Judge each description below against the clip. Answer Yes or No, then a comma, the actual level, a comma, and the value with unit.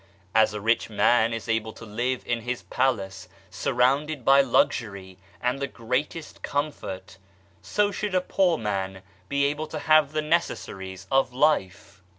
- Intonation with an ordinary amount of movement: No, wide, 5.8 semitones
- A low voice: Yes, low, 125 Hz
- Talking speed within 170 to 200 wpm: No, average, 155 wpm